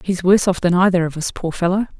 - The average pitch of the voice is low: No, medium, 180 Hz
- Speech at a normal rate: No, fast, 270 wpm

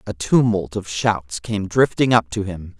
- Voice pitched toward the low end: Yes, low, 100 Hz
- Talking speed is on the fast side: No, average, 195 wpm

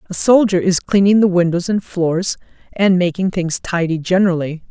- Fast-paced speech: No, average, 165 wpm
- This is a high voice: No, medium, 180 Hz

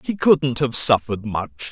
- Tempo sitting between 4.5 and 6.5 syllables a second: Yes, 5.0 syllables/s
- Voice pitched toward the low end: Yes, low, 125 Hz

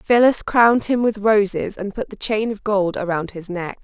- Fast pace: Yes, fast, 220 wpm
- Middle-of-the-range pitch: No, high, 210 Hz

